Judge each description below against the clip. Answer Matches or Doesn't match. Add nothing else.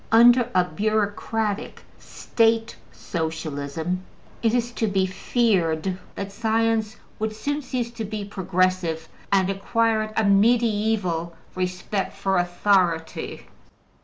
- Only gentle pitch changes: Doesn't match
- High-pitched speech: Matches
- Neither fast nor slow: Doesn't match